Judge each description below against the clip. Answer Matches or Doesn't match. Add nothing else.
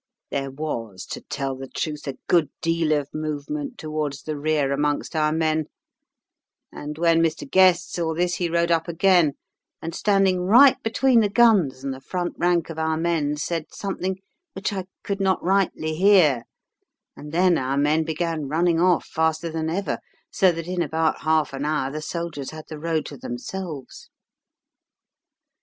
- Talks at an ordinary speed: Matches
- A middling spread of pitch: Matches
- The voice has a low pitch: Doesn't match